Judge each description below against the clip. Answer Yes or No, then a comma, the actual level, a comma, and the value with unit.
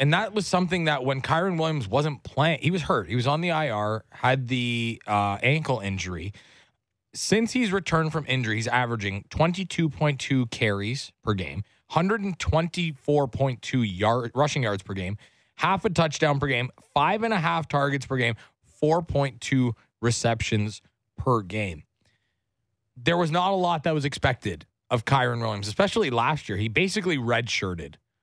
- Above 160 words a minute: No, average, 155 wpm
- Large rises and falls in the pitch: Yes, wide, 6.5 semitones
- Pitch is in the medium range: No, low, 130 Hz